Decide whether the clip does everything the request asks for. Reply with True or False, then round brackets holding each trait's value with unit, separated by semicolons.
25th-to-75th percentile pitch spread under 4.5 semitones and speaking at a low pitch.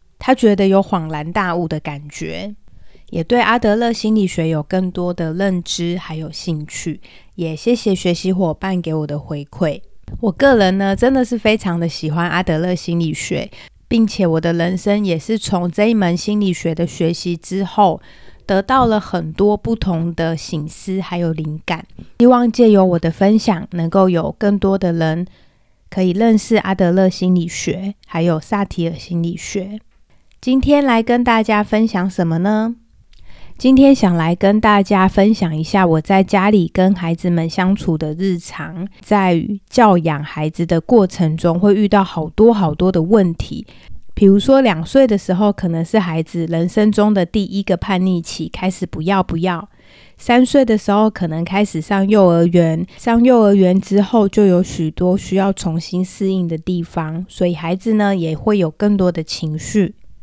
False (3.6 semitones; 185 Hz)